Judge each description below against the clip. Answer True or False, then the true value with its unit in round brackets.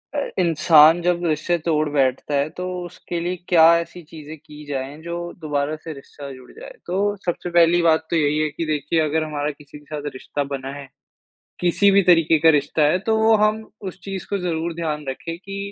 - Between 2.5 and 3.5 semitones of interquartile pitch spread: True (2.9 semitones)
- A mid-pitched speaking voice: True (160 Hz)